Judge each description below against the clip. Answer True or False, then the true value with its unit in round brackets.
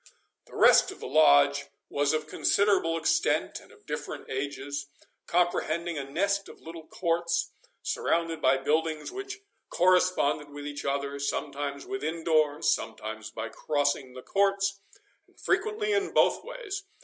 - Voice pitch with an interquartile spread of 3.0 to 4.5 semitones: False (5.5 semitones)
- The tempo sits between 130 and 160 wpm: True (140 wpm)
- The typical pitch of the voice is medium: True (160 Hz)